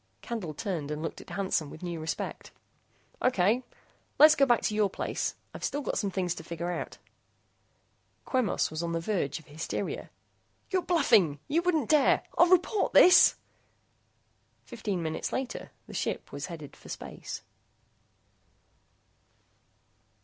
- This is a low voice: No, high, 195 Hz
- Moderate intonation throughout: No, wide, 8.1 semitones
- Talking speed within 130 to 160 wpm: Yes, average, 140 wpm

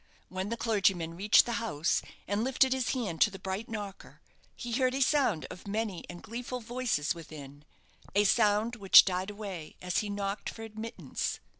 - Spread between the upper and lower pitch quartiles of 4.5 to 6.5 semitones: No, average, 3.8 semitones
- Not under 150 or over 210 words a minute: Yes, average, 175 wpm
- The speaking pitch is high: Yes, high, 205 Hz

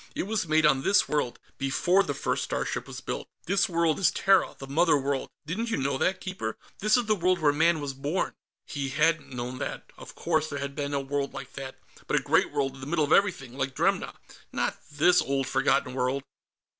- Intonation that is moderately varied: Yes, average, 4.3 semitones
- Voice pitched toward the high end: No, medium, 145 Hz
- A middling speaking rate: No, fast, 220 wpm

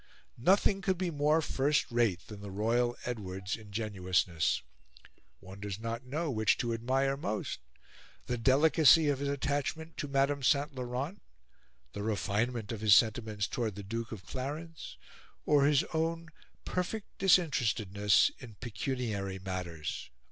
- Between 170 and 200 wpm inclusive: No, slow, 135 wpm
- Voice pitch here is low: Yes, low, 120 Hz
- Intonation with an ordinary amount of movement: No, wide, 5.8 semitones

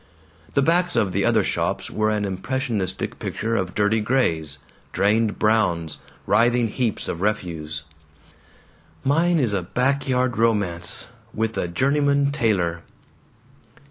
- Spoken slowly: Yes, slow, 125 wpm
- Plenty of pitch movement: Yes, wide, 5.8 semitones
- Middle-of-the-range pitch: No, low, 110 Hz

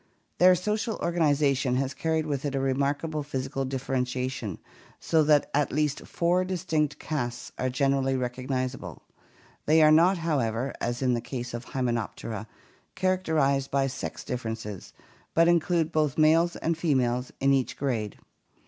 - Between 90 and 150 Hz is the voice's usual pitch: Yes, medium, 140 Hz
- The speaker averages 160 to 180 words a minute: No, average, 150 wpm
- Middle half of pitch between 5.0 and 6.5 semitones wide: No, average, 3.9 semitones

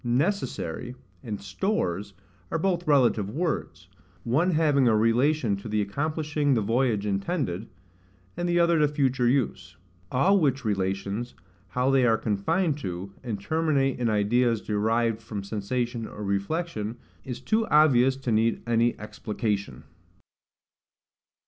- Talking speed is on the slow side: Yes, slow, 130 wpm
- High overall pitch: No, low, 120 Hz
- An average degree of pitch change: No, wide, 6.0 semitones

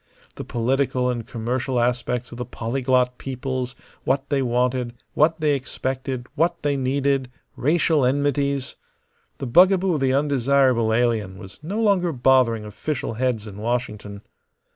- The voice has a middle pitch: No, low, 130 Hz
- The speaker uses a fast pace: No, average, 140 wpm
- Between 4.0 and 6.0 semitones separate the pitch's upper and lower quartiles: No, average, 2.7 semitones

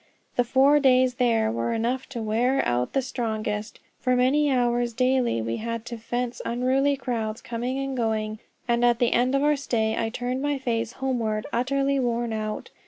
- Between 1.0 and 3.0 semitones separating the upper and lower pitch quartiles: Yes, narrow, 2.6 semitones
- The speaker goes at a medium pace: Yes, average, 180 wpm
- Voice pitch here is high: Yes, high, 240 Hz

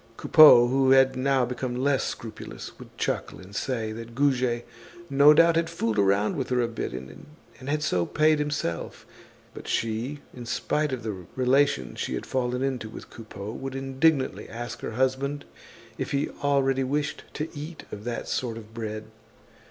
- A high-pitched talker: No, low, 130 Hz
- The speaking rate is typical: Yes, average, 170 wpm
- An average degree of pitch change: Yes, average, 3.8 semitones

